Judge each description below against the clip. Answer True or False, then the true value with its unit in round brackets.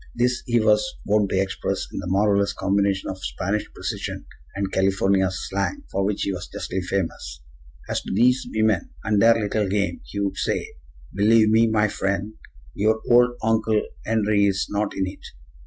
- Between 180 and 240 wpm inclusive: False (170 wpm)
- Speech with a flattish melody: True (2.2 semitones)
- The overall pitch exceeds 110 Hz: False (100 Hz)